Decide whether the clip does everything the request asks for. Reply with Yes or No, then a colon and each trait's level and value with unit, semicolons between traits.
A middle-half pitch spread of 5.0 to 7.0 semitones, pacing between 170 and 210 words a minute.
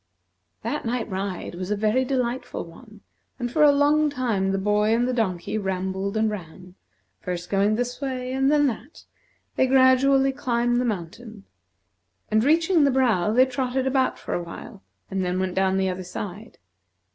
Yes: average, 5.3 semitones; average, 175 wpm